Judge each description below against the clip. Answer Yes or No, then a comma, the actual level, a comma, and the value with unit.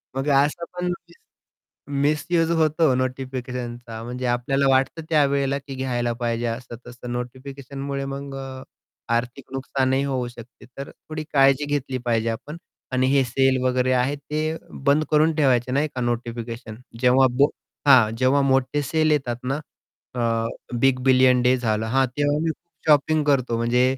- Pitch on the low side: Yes, low, 130 Hz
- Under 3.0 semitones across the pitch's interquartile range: Yes, narrow, 2.5 semitones